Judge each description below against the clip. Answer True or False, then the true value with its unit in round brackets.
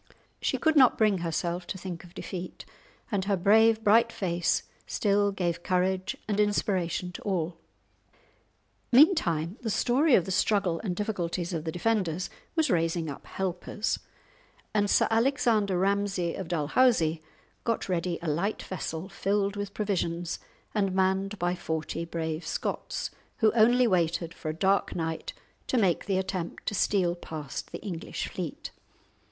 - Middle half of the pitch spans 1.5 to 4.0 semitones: True (3.4 semitones)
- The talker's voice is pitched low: False (190 Hz)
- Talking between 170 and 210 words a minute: False (150 wpm)